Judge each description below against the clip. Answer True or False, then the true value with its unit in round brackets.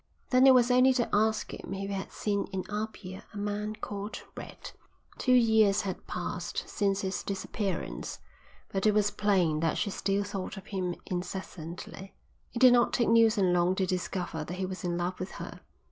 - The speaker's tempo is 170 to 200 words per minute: True (190 wpm)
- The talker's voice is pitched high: True (195 Hz)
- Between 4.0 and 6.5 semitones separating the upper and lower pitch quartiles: False (2.7 semitones)